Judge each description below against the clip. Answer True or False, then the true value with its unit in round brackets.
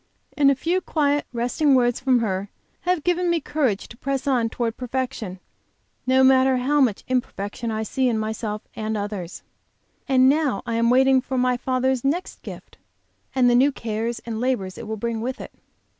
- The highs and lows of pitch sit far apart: False (3.0 semitones)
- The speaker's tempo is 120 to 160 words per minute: False (185 wpm)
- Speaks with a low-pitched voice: False (250 Hz)